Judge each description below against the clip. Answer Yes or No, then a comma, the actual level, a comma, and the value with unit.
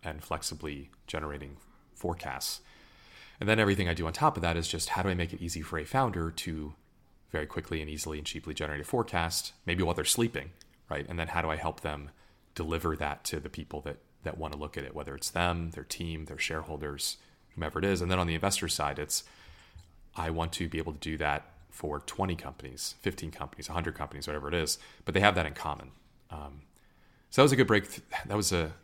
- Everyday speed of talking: No, fast, 230 wpm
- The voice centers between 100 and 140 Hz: No, very low, 80 Hz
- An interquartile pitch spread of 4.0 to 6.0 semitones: No, narrow, 2.5 semitones